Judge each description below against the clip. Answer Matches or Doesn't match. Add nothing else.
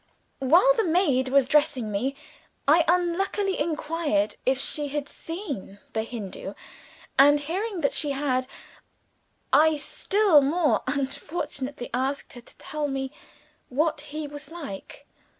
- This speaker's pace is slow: Matches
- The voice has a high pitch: Matches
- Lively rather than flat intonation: Doesn't match